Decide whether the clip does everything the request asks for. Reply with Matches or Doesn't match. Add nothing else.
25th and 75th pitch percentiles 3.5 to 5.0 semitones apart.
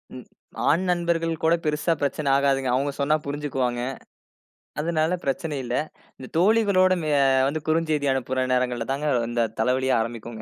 Matches